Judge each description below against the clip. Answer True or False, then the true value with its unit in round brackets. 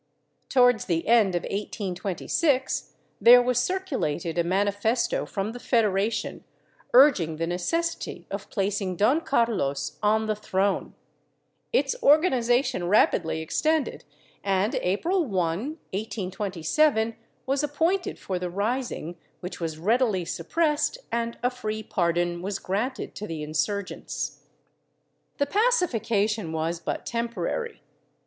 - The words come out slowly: True (115 wpm)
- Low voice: False (215 Hz)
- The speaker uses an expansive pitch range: True (5.8 semitones)